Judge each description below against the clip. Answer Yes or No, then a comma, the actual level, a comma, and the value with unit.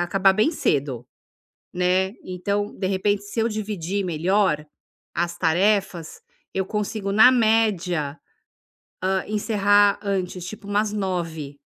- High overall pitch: Yes, high, 195 Hz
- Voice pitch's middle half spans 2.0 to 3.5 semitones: Yes, average, 2.9 semitones